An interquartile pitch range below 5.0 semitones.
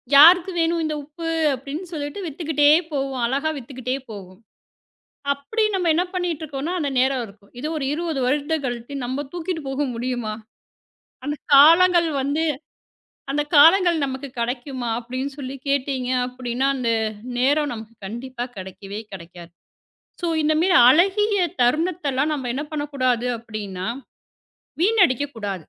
Yes: average, 4.3 semitones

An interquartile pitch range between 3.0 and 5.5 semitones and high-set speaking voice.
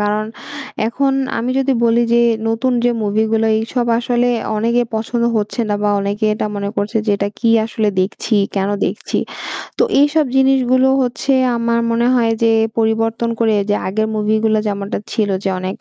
No: narrow, 2.4 semitones; high, 225 Hz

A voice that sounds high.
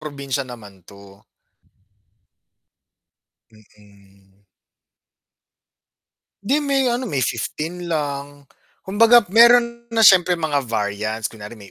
No: medium, 140 Hz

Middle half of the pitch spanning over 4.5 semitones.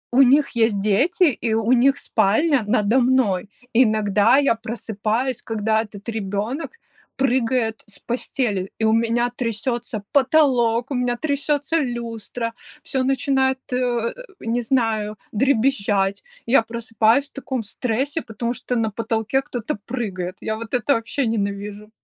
No: average, 3.2 semitones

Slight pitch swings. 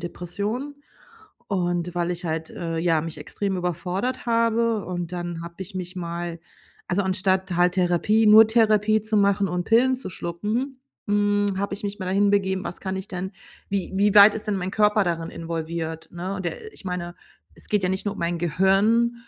No: average, 3.1 semitones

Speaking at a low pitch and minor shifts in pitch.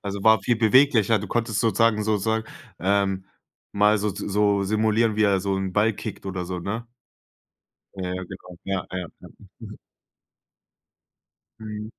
Yes: low, 105 Hz; narrow, 2.3 semitones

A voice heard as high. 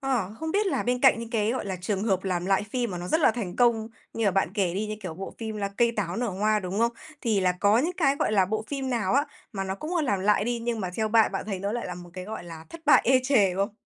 Yes: high, 215 Hz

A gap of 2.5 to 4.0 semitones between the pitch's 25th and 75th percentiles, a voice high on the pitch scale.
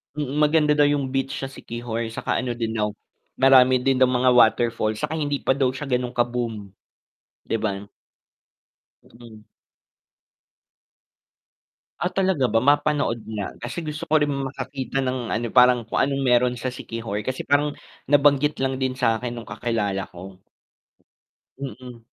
No: average, 3.2 semitones; low, 125 Hz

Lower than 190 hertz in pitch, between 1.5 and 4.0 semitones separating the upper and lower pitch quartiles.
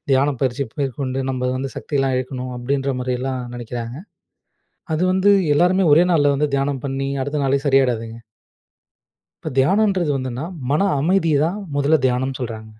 Yes: low, 135 Hz; narrow, 2.6 semitones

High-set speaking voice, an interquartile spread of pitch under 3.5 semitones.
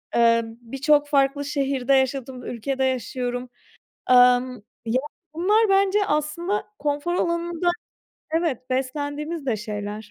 No: very high, 275 Hz; average, 4.0 semitones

